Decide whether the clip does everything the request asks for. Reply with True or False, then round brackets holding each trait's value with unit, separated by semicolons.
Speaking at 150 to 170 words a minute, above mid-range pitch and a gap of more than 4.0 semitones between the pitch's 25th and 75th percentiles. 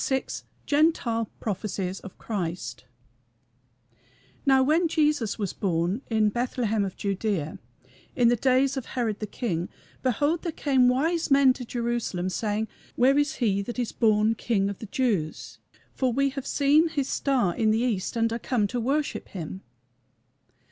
True (155 wpm; 235 Hz; 4.9 semitones)